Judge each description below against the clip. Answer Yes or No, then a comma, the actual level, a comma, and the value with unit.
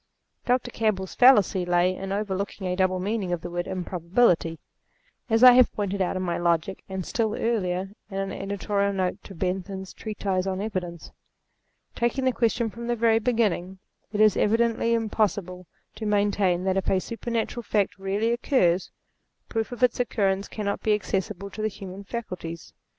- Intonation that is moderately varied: Yes, average, 3.3 semitones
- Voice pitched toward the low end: No, high, 200 Hz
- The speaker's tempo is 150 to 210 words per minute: Yes, average, 170 wpm